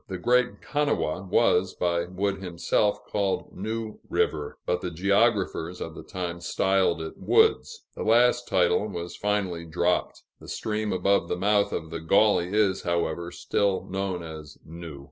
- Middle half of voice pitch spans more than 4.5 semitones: No, average, 3.3 semitones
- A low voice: Yes, very low, 95 Hz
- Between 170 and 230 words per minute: No, average, 155 wpm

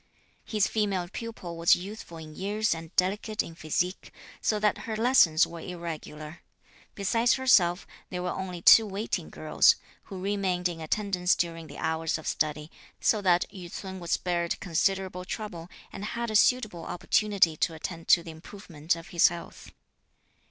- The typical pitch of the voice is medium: Yes, medium, 180 Hz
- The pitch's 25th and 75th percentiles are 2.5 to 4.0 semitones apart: Yes, average, 3.6 semitones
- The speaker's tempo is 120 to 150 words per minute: No, average, 160 wpm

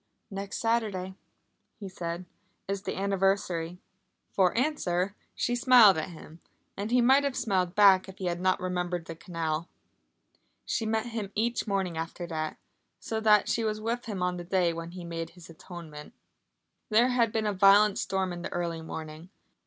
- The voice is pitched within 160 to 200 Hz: Yes, high, 190 Hz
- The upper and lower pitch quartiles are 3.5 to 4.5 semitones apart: Yes, average, 3.8 semitones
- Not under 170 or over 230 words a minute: Yes, average, 175 wpm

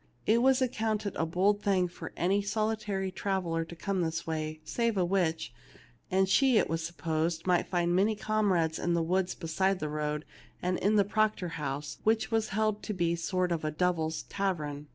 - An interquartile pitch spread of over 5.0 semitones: No, average, 3.8 semitones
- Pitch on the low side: No, medium, 180 Hz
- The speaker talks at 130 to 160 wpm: No, average, 195 wpm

